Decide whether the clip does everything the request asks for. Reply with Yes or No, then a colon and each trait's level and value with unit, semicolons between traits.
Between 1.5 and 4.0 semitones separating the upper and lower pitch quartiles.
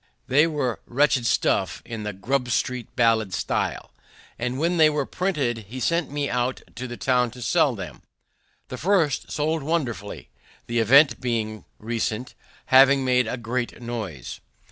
Yes: average, 3.5 semitones